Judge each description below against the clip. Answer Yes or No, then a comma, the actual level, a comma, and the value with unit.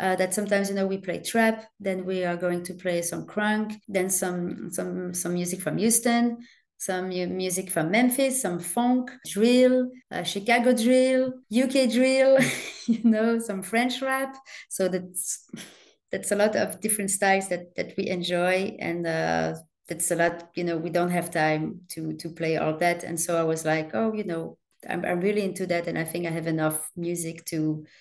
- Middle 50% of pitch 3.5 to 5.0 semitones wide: Yes, average, 4.7 semitones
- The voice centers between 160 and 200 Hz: Yes, medium, 185 Hz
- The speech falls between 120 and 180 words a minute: No, average, 190 wpm